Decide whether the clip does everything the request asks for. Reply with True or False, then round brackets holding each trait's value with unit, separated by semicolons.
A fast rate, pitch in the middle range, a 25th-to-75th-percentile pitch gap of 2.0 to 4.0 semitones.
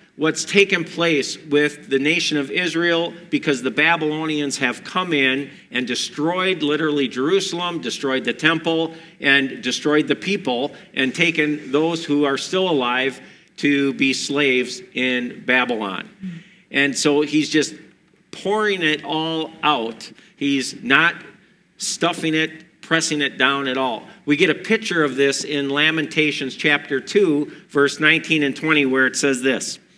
False (145 wpm; 150 Hz; 3.2 semitones)